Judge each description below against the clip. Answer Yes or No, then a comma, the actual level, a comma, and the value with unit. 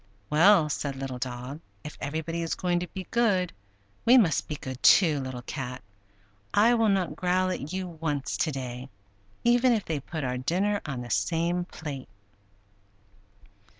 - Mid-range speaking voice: Yes, medium, 160 Hz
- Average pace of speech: Yes, average, 160 wpm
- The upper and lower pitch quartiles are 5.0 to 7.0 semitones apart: Yes, wide, 5.5 semitones